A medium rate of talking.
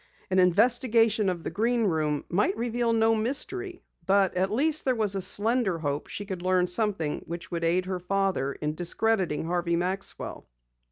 Yes: average, 170 wpm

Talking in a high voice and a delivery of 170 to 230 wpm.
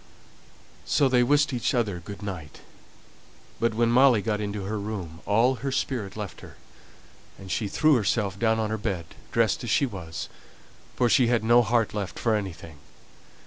No: low, 110 Hz; average, 175 wpm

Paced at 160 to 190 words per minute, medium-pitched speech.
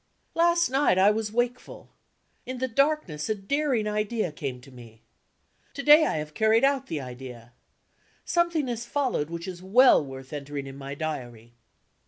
No: average, 165 wpm; high, 205 Hz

